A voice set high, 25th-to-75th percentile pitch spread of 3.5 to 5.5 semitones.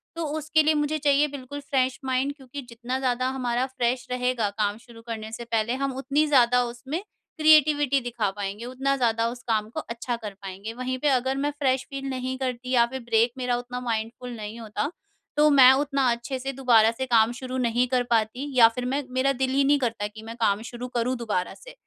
No: very high, 250 Hz; narrow, 2.6 semitones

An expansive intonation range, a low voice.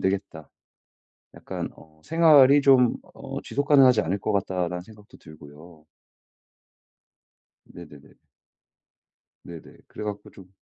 Yes: wide, 6.9 semitones; low, 100 Hz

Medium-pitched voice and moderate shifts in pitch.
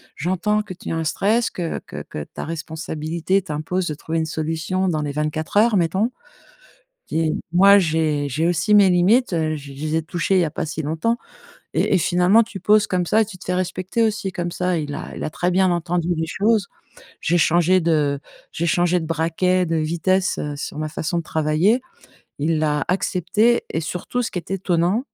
Yes: medium, 175 Hz; average, 3.1 semitones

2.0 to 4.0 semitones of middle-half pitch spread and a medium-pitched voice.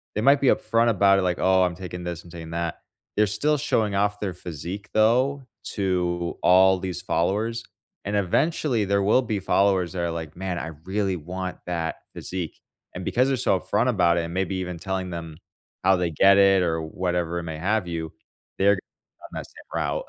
No: average, 2.9 semitones; very low, 95 Hz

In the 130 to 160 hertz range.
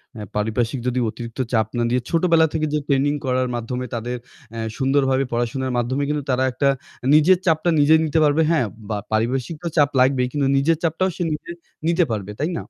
Yes: low, 135 Hz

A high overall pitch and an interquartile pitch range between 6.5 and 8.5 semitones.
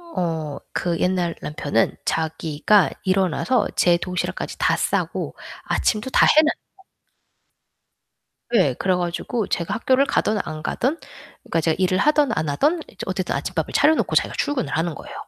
No: medium, 180 Hz; wide, 6.8 semitones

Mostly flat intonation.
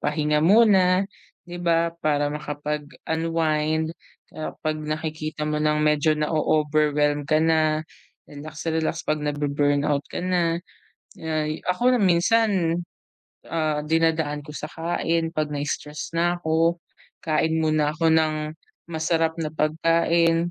Yes: narrow, 1.6 semitones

